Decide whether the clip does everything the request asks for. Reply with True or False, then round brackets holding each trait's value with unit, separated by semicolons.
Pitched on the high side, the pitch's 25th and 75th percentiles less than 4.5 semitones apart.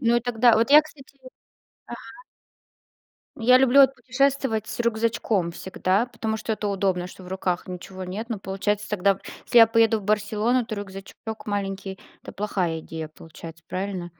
True (210 Hz; 3.6 semitones)